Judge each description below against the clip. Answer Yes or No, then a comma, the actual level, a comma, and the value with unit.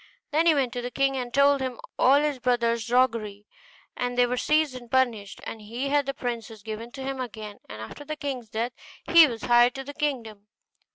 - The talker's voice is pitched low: No, high, 245 Hz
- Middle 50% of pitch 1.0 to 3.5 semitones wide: Yes, average, 3.1 semitones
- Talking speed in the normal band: No, fast, 215 wpm